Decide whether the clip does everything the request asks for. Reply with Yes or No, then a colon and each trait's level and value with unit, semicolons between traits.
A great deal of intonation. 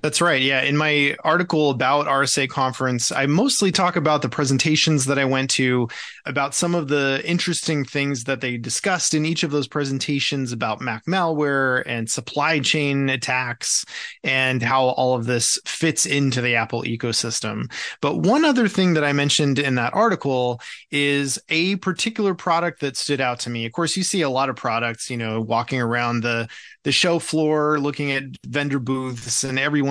No: average, 3.4 semitones